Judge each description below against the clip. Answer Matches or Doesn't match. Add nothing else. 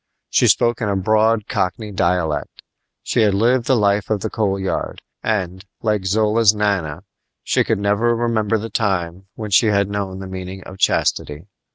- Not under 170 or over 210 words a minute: Matches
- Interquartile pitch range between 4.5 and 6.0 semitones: Doesn't match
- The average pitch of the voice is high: Doesn't match